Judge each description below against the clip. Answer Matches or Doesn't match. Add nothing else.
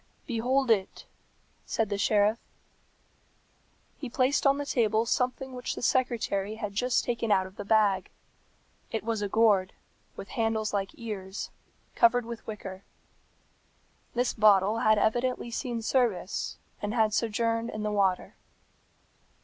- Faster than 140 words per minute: Doesn't match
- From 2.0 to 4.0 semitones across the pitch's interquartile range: Matches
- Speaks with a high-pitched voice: Matches